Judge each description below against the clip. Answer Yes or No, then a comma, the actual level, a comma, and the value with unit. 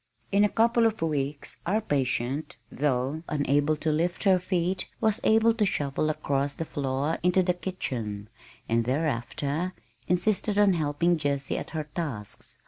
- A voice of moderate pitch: Yes, medium, 155 Hz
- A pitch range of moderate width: Yes, average, 4.8 semitones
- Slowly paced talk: No, average, 150 wpm